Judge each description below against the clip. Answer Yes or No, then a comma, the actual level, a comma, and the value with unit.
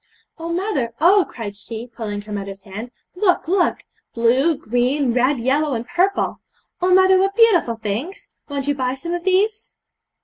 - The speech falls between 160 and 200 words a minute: Yes, average, 165 wpm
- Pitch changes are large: Yes, wide, 7.7 semitones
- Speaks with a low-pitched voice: No, very high, 280 Hz